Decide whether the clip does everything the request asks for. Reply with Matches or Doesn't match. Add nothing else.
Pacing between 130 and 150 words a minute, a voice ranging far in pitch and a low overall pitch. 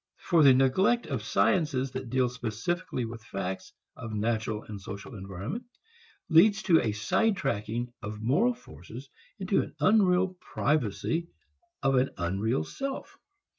Matches